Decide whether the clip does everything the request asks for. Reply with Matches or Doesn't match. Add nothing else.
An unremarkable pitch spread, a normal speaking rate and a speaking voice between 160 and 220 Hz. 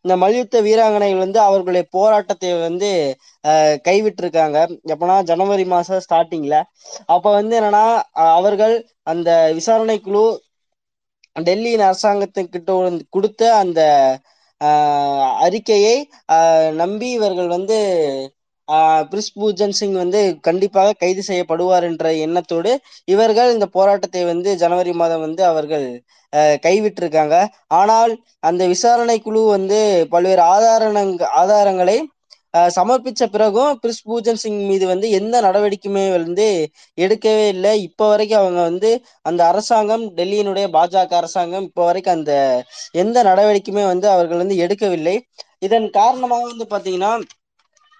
Matches